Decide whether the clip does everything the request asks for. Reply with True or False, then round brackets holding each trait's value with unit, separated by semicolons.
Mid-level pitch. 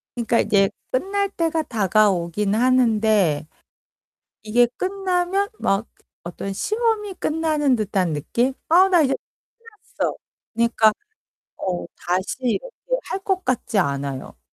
False (235 Hz)